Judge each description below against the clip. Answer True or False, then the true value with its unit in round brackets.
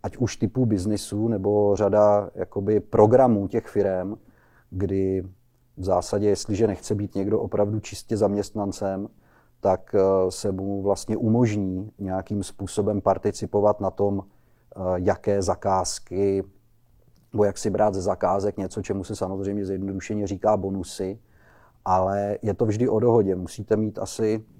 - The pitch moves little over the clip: True (1.7 semitones)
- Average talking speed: True (130 wpm)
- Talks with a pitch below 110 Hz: True (100 Hz)